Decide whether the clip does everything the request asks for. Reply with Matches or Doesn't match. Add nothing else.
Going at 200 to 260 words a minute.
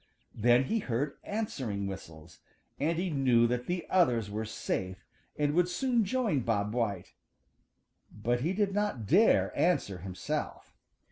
Doesn't match